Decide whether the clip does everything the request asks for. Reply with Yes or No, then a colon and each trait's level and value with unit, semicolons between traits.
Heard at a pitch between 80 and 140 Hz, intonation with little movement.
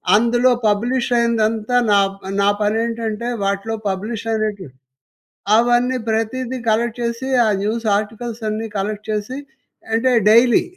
No: high, 225 Hz; narrow, 2.0 semitones